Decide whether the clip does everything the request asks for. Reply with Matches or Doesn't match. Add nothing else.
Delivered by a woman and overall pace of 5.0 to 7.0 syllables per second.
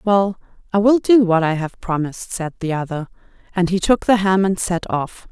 Matches